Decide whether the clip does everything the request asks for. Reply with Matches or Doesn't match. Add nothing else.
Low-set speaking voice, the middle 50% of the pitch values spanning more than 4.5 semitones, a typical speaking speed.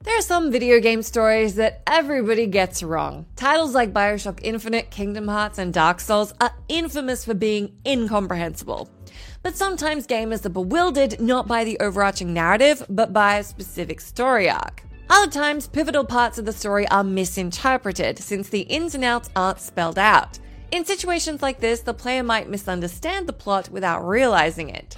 Doesn't match